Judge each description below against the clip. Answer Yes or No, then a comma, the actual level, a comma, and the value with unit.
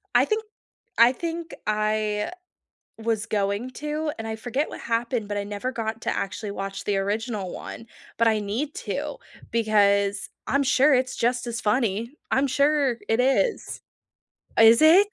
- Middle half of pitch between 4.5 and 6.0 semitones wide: No, average, 3.9 semitones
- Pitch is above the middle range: Yes, high, 230 Hz